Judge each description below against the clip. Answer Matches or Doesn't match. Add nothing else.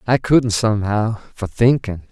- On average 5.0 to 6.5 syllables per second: Doesn't match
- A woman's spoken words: Doesn't match